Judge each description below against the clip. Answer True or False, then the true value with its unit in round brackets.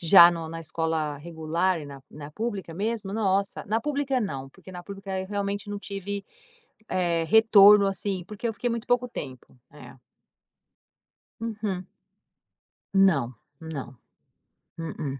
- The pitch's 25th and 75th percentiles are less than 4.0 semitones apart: False (4.3 semitones)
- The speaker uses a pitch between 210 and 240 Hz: False (190 Hz)